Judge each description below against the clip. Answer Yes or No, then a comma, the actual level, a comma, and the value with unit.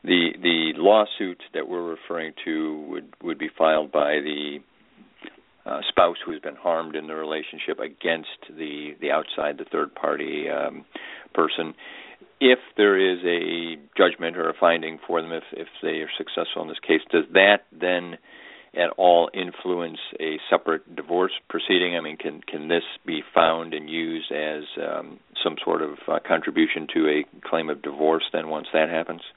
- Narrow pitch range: Yes, narrow, 2.0 semitones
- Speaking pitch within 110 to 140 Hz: No, very low, 80 Hz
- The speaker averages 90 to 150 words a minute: No, average, 170 wpm